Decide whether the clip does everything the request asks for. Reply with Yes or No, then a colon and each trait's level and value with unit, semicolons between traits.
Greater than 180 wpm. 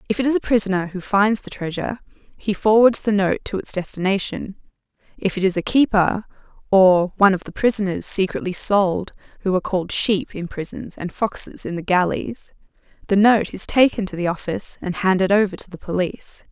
Yes: average, 190 wpm